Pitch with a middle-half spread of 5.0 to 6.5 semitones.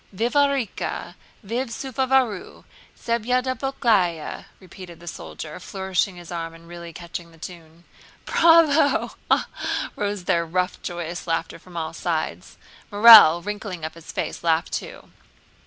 Yes: wide, 5.6 semitones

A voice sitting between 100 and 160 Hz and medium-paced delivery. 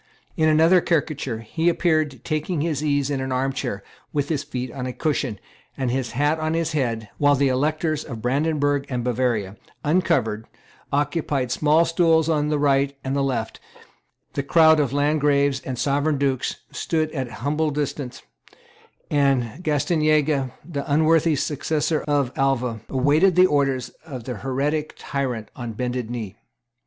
Yes: medium, 140 Hz; average, 150 wpm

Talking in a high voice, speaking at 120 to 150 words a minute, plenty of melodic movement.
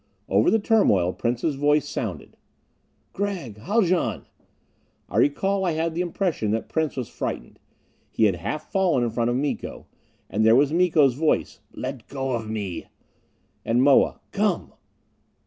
No: medium, 140 Hz; average, 145 wpm; wide, 6.8 semitones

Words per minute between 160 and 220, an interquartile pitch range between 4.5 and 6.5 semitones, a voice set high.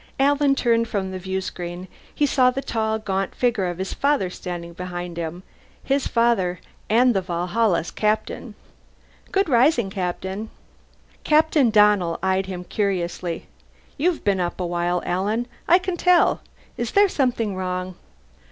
No: average, 145 wpm; wide, 5.5 semitones; high, 195 Hz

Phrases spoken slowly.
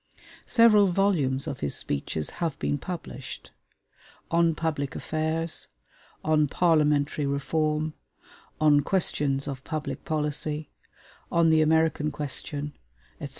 Yes: slow, 110 wpm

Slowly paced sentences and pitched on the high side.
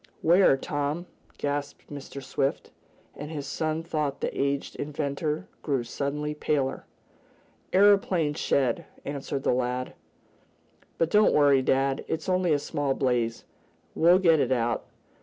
No: slow, 130 wpm; medium, 145 Hz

